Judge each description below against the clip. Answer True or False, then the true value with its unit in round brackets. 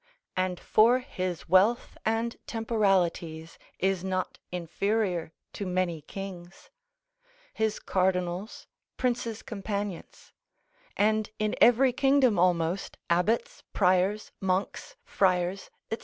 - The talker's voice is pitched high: True (195 Hz)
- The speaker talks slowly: True (95 wpm)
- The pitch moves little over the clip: False (3.5 semitones)